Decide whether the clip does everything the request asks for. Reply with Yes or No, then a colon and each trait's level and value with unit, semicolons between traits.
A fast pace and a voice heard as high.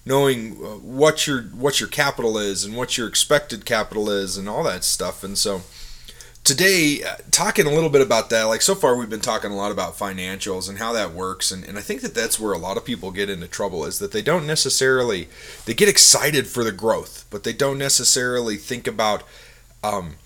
No: fast, 215 wpm; low, 115 Hz